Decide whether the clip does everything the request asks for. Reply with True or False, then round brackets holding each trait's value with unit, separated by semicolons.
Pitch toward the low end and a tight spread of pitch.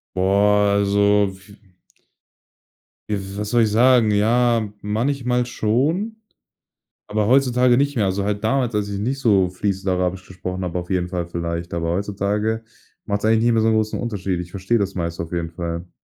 False (105 Hz; 3.6 semitones)